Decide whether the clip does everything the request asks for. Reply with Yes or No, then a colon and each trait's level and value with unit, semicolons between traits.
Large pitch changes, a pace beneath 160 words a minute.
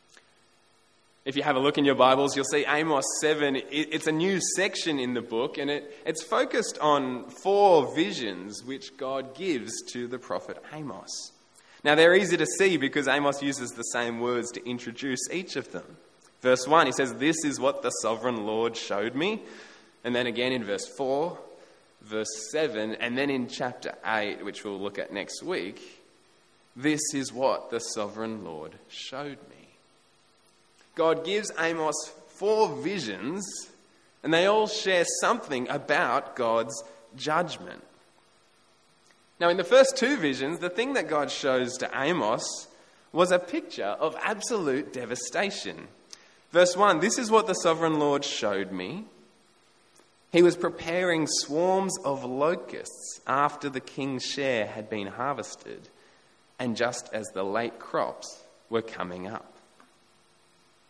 Yes: wide, 6.2 semitones; average, 150 wpm